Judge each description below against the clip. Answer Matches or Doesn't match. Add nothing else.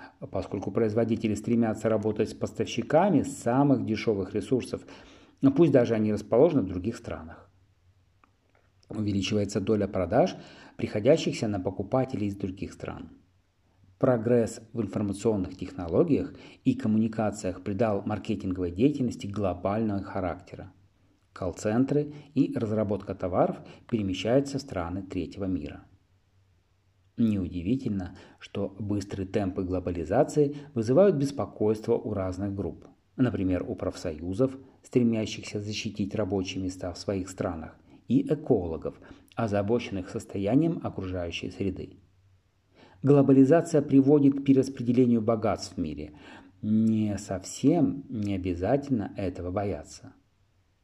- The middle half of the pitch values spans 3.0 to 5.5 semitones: Matches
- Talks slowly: Matches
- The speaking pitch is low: Matches